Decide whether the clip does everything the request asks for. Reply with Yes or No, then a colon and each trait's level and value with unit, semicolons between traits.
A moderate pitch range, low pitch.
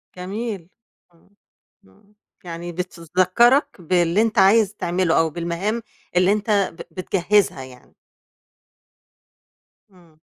No: average, 3.5 semitones; medium, 180 Hz